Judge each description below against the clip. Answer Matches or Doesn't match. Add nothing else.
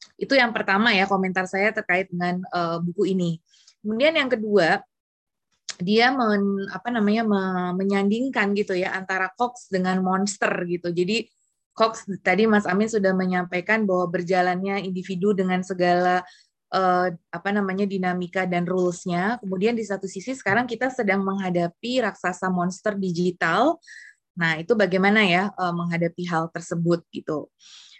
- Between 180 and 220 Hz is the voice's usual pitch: Matches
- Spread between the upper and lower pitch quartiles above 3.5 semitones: Doesn't match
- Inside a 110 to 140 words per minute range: Matches